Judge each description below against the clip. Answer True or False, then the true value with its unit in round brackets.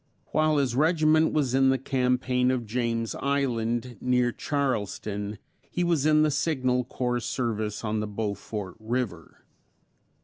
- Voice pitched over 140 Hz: False (125 Hz)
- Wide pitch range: False (3.8 semitones)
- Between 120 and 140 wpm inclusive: True (135 wpm)